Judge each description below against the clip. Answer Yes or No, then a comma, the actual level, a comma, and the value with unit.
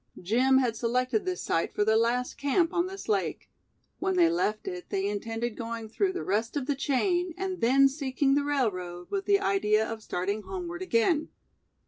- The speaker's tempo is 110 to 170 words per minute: No, average, 185 wpm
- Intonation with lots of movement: Yes, wide, 7.9 semitones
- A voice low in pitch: No, very high, 255 Hz